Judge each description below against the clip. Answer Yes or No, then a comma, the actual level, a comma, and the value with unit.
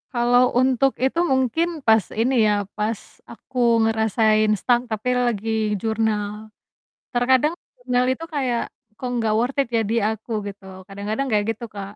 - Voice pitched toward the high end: Yes, high, 230 Hz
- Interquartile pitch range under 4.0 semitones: Yes, average, 2.8 semitones